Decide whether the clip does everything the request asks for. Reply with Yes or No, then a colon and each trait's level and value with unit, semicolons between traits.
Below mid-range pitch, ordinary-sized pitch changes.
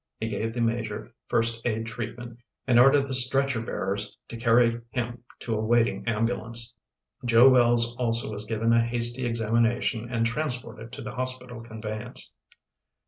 No: low, 115 Hz; narrow, 1.1 semitones